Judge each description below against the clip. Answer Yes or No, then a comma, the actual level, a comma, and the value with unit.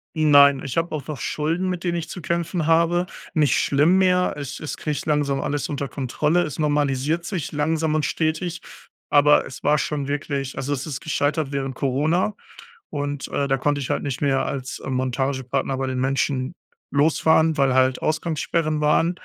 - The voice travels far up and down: No, average, 2.7 semitones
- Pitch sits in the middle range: Yes, medium, 145 Hz